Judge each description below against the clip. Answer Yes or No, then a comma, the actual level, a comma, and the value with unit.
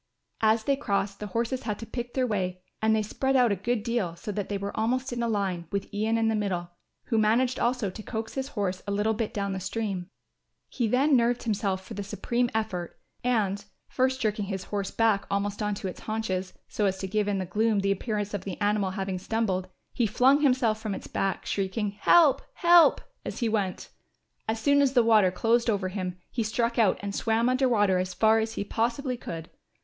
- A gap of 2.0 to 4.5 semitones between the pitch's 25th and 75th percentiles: Yes, average, 3.0 semitones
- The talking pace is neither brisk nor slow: No, fast, 220 wpm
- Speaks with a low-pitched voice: No, high, 215 Hz